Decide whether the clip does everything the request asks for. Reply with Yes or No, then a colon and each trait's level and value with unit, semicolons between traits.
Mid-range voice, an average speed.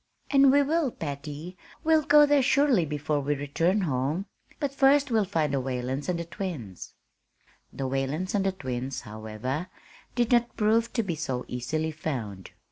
Yes: medium, 160 Hz; average, 165 wpm